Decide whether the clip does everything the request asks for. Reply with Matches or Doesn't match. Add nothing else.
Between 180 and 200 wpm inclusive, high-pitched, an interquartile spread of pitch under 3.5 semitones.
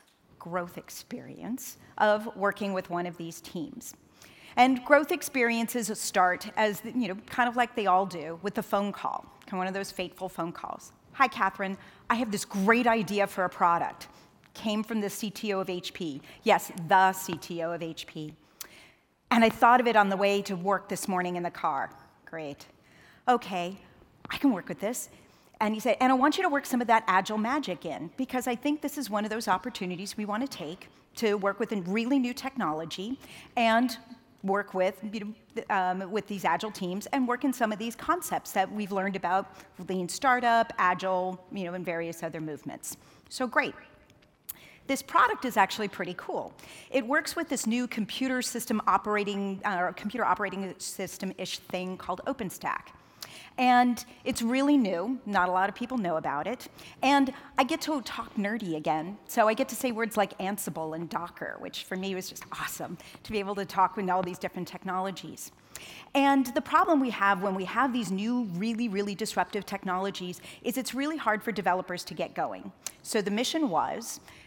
Doesn't match